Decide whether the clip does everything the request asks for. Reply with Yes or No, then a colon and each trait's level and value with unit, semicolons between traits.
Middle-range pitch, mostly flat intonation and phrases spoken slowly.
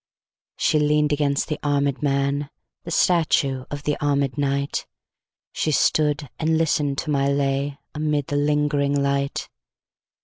Yes: medium, 145 Hz; narrow, 1.2 semitones; slow, 115 wpm